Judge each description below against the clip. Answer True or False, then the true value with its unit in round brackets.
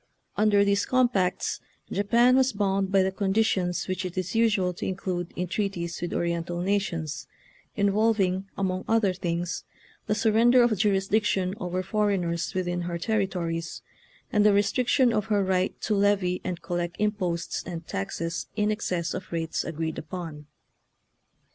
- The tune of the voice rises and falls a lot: False (3.0 semitones)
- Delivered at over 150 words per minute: False (145 wpm)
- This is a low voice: False (190 Hz)